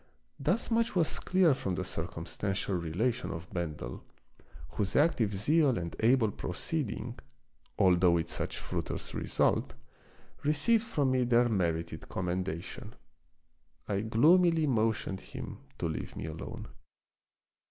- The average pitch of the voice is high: No, low, 110 Hz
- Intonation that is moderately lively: No, wide, 8.7 semitones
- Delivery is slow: Yes, slow, 120 wpm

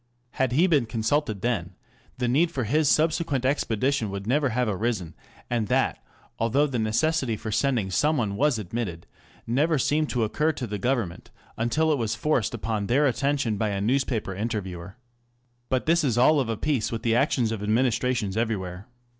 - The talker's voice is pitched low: Yes, low, 120 Hz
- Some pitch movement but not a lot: Yes, average, 4.5 semitones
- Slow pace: No, average, 180 wpm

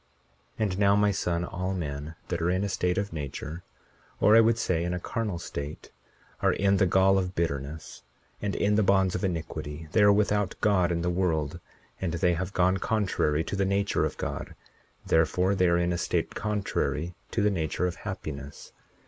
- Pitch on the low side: Yes, very low, 90 Hz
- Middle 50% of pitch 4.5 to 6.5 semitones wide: No, average, 3.1 semitones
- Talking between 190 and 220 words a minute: Yes, average, 200 wpm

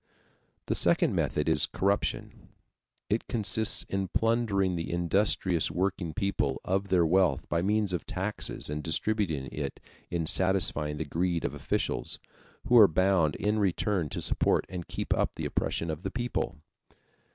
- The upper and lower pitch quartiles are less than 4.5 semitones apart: Yes, average, 3.6 semitones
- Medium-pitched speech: No, very low, 95 Hz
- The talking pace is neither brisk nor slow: Yes, average, 150 wpm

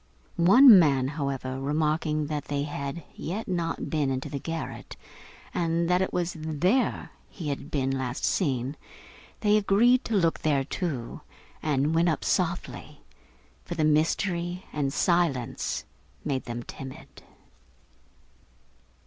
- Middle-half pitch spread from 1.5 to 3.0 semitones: No, average, 4.0 semitones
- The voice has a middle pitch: Yes, medium, 155 Hz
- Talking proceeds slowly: Yes, slow, 130 wpm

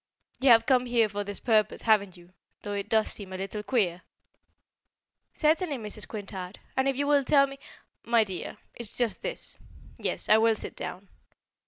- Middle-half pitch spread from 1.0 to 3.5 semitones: No, average, 4.1 semitones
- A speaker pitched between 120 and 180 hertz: No, high, 220 Hz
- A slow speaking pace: No, average, 185 wpm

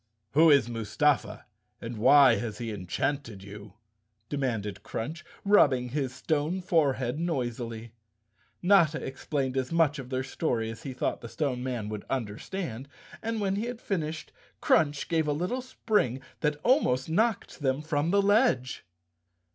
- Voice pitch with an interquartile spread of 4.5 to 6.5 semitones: Yes, wide, 5.4 semitones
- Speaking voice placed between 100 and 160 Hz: Yes, medium, 140 Hz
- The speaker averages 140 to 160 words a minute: Yes, average, 145 wpm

